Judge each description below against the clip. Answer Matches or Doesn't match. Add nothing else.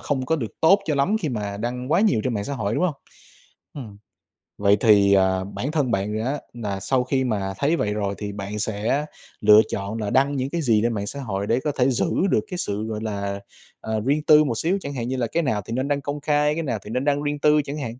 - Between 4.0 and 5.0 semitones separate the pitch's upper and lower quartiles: Doesn't match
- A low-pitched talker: Matches